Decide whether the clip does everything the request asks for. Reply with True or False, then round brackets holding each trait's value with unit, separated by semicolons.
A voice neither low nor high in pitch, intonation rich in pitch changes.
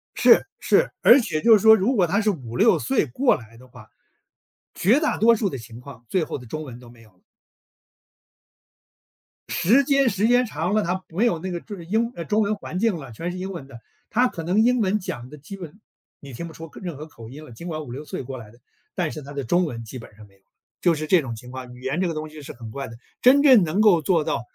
True (165 Hz; 8.0 semitones)